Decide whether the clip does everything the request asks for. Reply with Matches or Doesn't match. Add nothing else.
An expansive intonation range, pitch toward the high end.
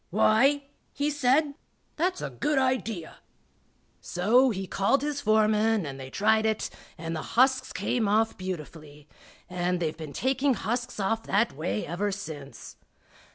Matches